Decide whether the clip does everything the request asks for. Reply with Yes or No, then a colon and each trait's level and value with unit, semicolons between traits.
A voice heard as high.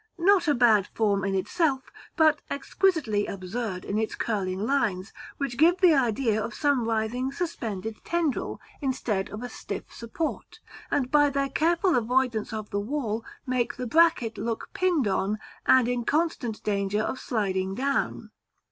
Yes: high, 240 Hz